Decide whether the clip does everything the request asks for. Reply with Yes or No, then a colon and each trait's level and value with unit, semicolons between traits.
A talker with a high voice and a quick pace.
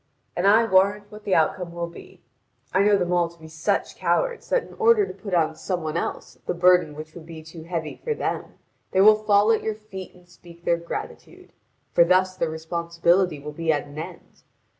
No: medium, 175 Hz; fast, 215 wpm